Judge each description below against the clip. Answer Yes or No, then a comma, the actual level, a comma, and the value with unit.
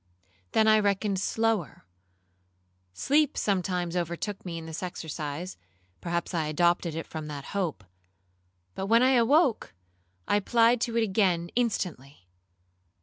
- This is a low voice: No, medium, 185 Hz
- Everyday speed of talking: No, slow, 130 wpm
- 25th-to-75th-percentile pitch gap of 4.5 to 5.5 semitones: Yes, average, 5.1 semitones